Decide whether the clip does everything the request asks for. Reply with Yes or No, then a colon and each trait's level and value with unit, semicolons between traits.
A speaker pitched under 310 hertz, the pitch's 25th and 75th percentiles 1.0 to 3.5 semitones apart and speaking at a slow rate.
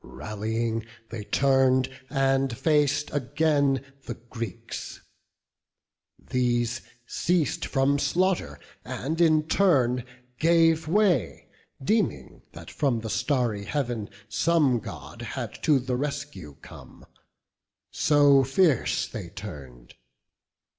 No: low, 135 Hz; average, 4.6 semitones; slow, 100 wpm